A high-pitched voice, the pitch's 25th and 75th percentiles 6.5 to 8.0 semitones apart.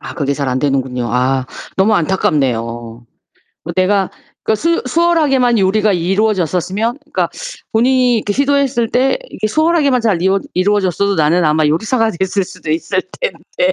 Yes: high, 200 Hz; wide, 7.1 semitones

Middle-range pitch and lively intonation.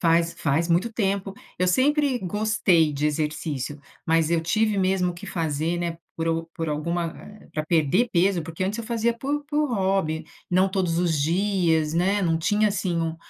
No: medium, 175 Hz; average, 3.8 semitones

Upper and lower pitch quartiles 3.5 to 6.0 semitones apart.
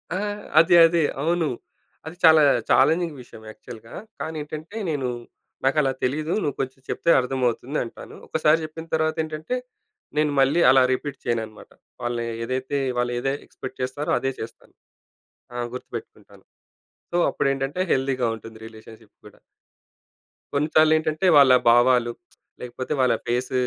Yes: average, 4.0 semitones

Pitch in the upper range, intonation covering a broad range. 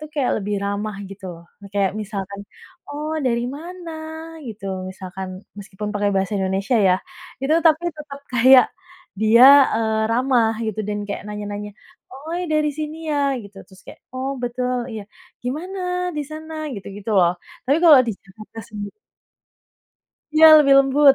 Yes: high, 230 Hz; wide, 5.9 semitones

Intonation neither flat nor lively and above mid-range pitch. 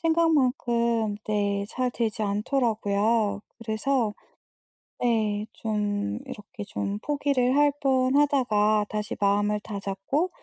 Yes: average, 3.8 semitones; high, 220 Hz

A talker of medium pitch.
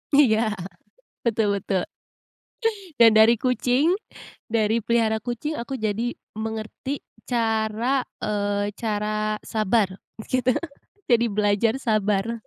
No: high, 220 Hz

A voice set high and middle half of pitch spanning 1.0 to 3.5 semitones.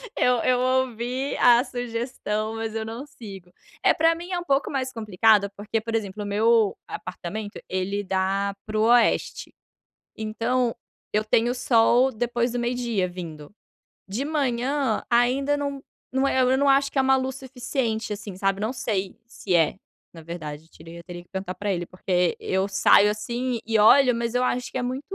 No: high, 225 Hz; average, 4.1 semitones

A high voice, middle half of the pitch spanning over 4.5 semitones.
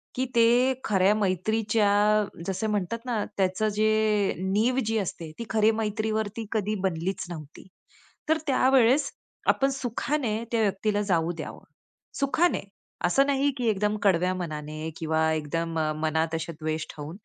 Yes: high, 210 Hz; average, 4.9 semitones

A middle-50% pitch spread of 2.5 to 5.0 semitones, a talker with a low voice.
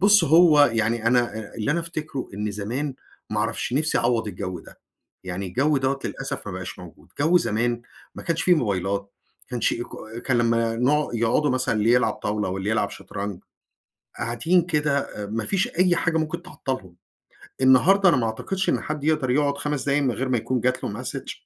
No: wide, 5.5 semitones; low, 125 Hz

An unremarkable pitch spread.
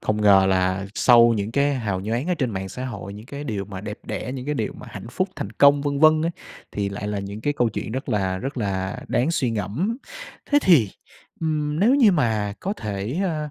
No: wide, 6.4 semitones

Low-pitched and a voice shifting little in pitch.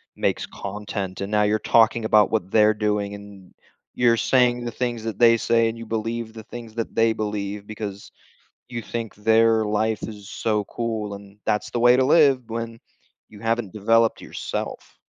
Yes: low, 110 Hz; narrow, 1.8 semitones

